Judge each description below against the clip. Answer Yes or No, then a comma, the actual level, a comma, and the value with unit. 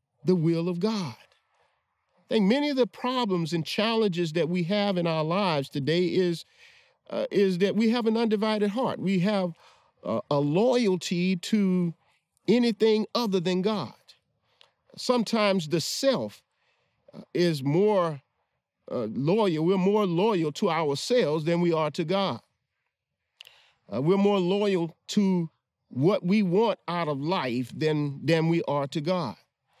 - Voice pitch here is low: No, medium, 185 Hz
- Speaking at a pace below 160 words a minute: Yes, average, 145 wpm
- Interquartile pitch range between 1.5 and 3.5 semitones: No, average, 4.3 semitones